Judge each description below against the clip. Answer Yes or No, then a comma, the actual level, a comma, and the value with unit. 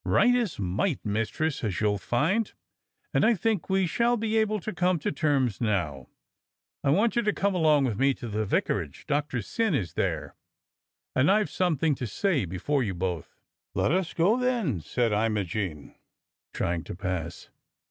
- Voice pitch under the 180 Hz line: Yes, medium, 140 Hz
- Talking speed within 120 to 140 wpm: No, average, 170 wpm